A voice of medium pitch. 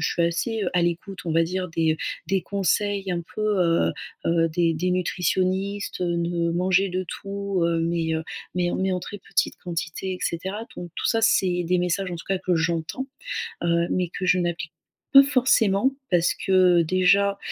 Yes: medium, 180 Hz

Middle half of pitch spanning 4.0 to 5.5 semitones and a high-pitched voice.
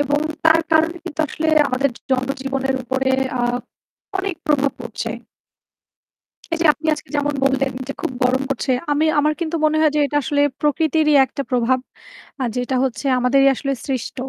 No: narrow, 2.6 semitones; very high, 275 Hz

